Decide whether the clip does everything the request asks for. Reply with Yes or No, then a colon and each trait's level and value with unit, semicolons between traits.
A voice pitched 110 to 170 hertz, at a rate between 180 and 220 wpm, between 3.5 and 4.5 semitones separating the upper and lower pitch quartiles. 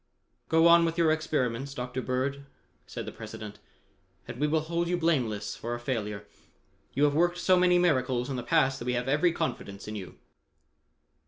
No: medium, 140 Hz; average, 185 wpm; average, 5.1 semitones